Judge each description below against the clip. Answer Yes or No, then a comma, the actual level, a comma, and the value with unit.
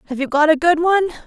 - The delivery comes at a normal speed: No, fast, 285 wpm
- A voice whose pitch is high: Yes, very high, 315 Hz